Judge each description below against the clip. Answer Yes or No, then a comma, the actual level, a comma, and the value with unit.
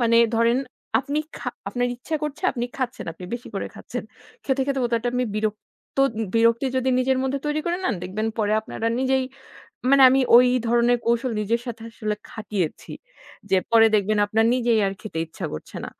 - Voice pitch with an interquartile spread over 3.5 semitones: No, average, 3.2 semitones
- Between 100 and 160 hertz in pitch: No, high, 235 Hz